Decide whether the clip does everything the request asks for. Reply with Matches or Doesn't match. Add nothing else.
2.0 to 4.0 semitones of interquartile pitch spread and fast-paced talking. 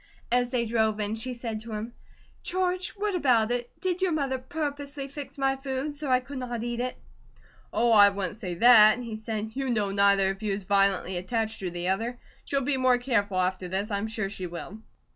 Doesn't match